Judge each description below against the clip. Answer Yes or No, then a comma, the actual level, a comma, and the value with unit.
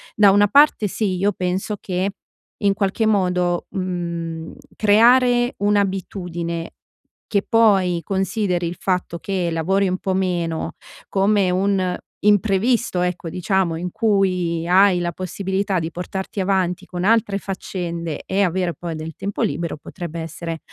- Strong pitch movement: No, narrow, 2.5 semitones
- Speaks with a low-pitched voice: No, medium, 185 Hz